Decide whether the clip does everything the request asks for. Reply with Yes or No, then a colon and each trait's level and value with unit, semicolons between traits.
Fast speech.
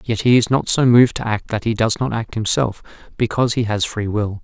Yes: fast, 255 wpm